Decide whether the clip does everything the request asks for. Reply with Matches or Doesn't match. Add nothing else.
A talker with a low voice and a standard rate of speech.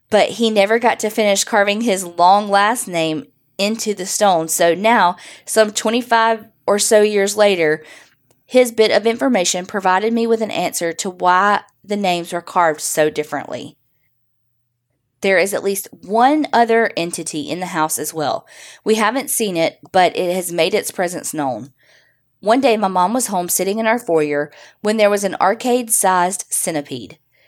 Doesn't match